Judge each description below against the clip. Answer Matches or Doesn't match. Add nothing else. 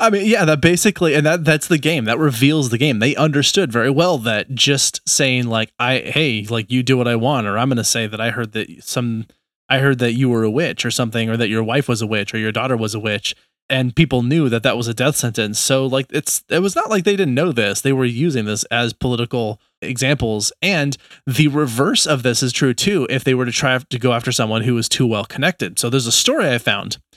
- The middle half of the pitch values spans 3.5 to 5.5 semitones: Matches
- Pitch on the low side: Matches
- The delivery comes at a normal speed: Doesn't match